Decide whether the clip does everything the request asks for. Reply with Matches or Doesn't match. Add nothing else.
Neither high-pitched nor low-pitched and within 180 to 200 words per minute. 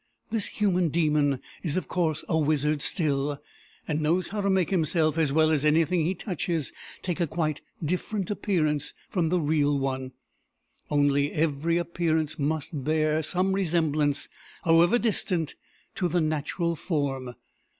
Doesn't match